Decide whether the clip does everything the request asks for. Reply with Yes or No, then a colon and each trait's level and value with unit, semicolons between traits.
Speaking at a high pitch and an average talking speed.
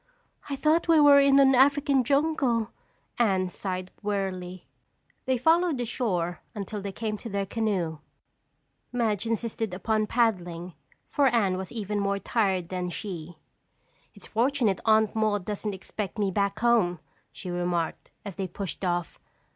Yes: high, 210 Hz; average, 145 wpm